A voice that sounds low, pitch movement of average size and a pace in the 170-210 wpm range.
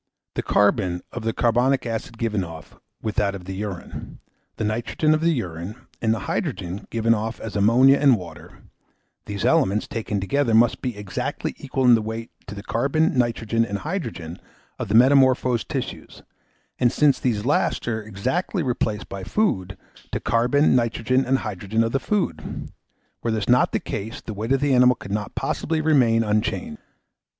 Yes: low, 115 Hz; average, 3.9 semitones; average, 175 wpm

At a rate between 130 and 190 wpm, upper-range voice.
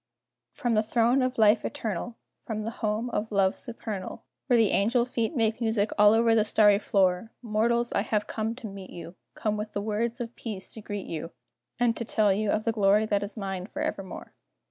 No: fast, 205 wpm; high, 215 Hz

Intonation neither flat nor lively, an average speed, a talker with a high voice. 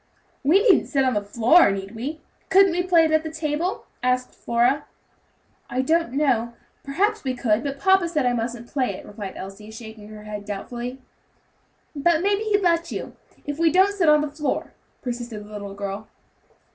No: wide, 7.0 semitones; average, 185 wpm; very high, 265 Hz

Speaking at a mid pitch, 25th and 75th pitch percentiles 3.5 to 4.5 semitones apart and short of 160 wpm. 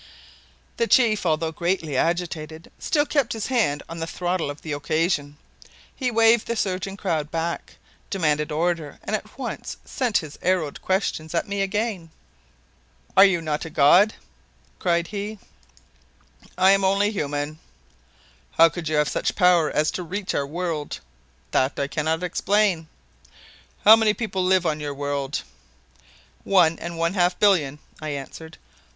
Yes: medium, 170 Hz; average, 4.2 semitones; average, 150 wpm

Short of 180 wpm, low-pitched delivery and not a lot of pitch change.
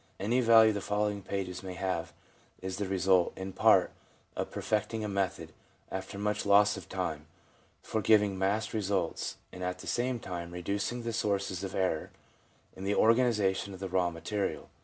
Yes: average, 170 wpm; low, 100 Hz; narrow, 2.1 semitones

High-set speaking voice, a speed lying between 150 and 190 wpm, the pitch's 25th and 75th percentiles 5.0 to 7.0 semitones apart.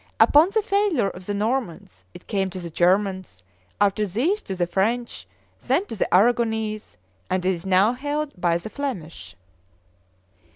Yes: high, 205 Hz; average, 160 wpm; wide, 5.4 semitones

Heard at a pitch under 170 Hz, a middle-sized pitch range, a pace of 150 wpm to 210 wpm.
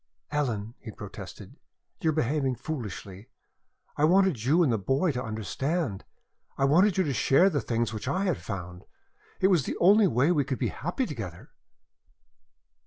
No: low, 135 Hz; wide, 7.1 semitones; average, 170 wpm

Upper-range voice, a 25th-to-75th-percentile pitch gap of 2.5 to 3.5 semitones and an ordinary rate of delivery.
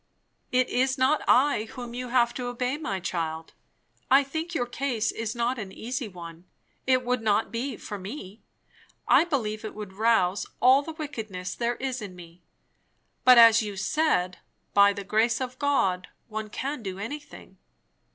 No: high, 235 Hz; average, 4.3 semitones; average, 170 wpm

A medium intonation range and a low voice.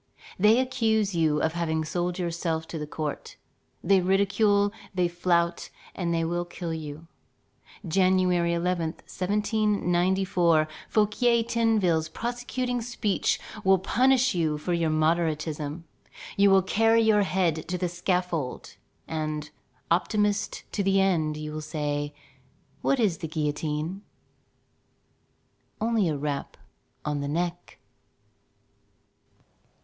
No: average, 4.1 semitones; medium, 175 Hz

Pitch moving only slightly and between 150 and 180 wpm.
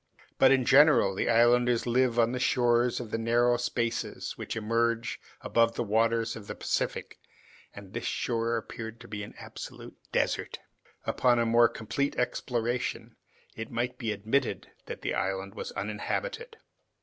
Yes: narrow, 1.5 semitones; average, 155 wpm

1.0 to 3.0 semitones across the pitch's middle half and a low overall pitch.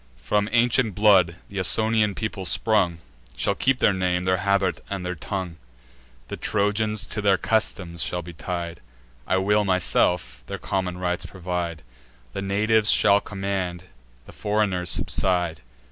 Yes: average, 2.7 semitones; very low, 95 Hz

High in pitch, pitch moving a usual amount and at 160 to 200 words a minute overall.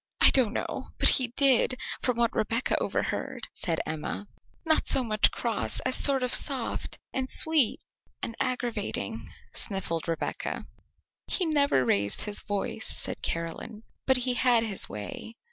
No: high, 235 Hz; average, 4.3 semitones; average, 145 wpm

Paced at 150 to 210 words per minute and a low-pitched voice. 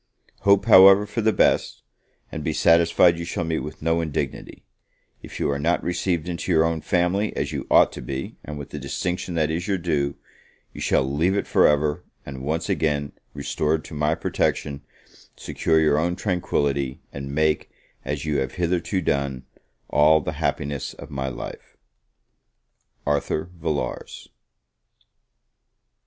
Yes: average, 155 wpm; very low, 80 Hz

